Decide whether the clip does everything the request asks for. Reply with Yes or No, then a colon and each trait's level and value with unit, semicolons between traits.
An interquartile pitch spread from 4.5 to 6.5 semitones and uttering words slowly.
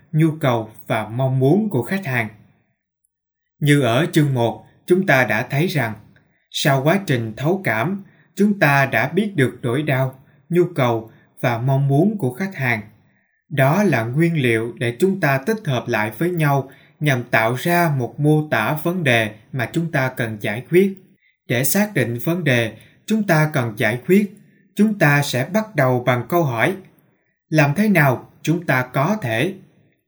No: wide, 5.6 semitones; average, 175 wpm